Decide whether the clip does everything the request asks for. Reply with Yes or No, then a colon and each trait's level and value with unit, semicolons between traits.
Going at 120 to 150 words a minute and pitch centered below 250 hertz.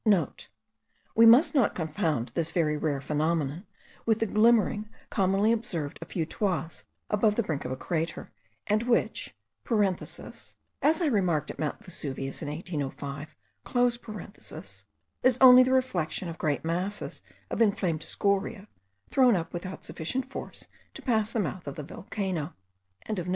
Yes: average, 140 wpm; high, 190 Hz